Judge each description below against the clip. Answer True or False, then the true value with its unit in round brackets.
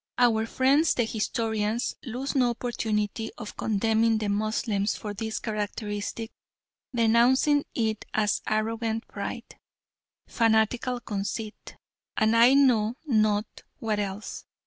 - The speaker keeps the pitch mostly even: True (1.9 semitones)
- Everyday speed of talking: False (110 wpm)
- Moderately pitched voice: False (220 Hz)